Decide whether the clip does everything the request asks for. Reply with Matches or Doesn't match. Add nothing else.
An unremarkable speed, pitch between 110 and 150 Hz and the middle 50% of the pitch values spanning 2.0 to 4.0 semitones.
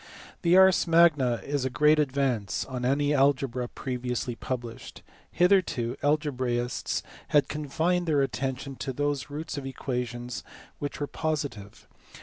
Doesn't match